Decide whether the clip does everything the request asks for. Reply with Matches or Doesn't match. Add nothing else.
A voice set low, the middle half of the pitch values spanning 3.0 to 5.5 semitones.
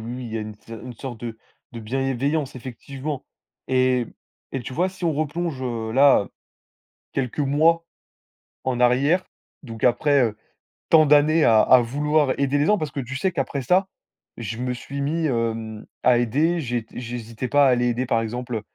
Matches